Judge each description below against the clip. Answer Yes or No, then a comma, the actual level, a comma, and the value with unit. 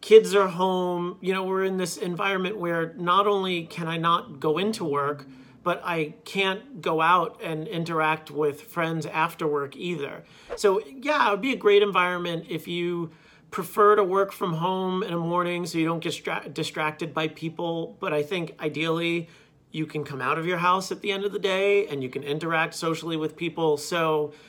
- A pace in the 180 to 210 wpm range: Yes, average, 200 wpm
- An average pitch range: Yes, average, 3.2 semitones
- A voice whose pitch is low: No, medium, 170 Hz